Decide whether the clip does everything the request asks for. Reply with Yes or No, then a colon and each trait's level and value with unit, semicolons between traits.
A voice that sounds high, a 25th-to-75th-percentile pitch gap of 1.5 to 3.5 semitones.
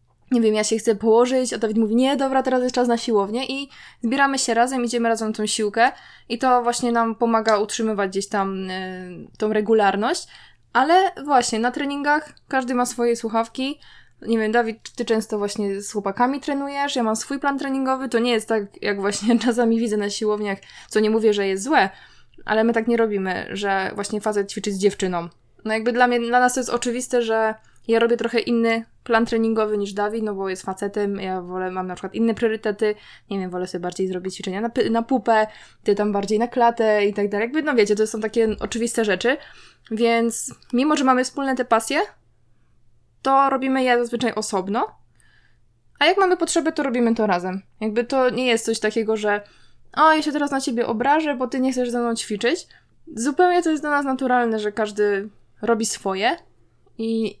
Yes: high, 230 Hz; average, 3.1 semitones